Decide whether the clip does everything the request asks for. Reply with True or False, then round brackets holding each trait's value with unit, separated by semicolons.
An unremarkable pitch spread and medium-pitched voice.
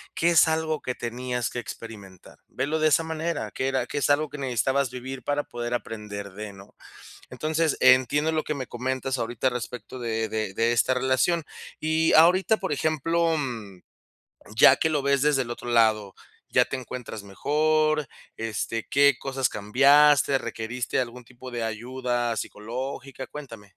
False (4.2 semitones; 130 Hz)